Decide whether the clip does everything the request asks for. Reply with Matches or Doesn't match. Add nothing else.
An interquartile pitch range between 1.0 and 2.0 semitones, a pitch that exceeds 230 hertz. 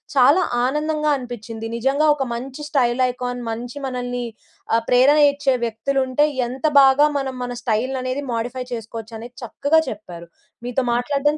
Doesn't match